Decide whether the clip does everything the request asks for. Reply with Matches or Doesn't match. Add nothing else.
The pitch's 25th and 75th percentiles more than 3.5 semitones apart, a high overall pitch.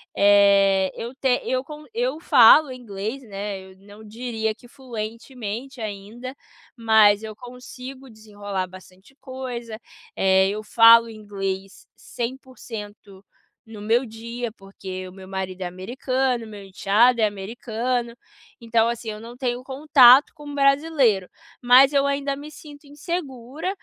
Matches